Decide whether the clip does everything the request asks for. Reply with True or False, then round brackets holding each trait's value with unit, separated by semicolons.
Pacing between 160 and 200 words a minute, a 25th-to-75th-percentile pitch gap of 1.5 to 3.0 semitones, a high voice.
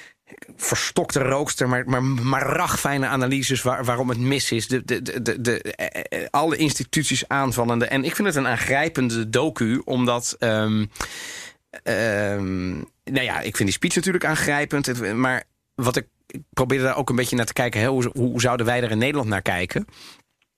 False (180 wpm; 2.5 semitones; 125 Hz)